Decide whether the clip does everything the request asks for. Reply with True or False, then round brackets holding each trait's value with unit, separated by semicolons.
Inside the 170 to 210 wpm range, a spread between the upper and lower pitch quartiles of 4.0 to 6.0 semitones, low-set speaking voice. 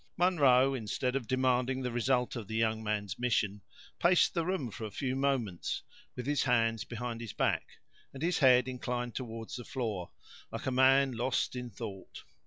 False (180 wpm; 2.7 semitones; 125 Hz)